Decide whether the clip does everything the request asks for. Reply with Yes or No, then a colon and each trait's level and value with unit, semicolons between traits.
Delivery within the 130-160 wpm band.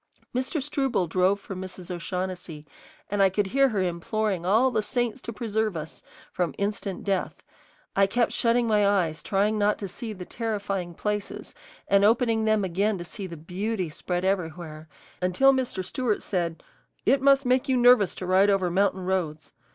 No: average, 175 wpm